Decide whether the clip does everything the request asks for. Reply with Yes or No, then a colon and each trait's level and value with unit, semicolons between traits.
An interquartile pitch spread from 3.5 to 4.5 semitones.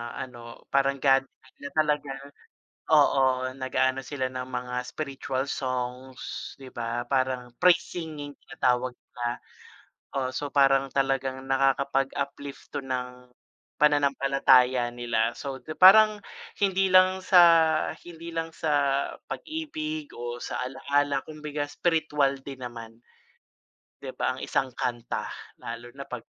No: average, 2.7 semitones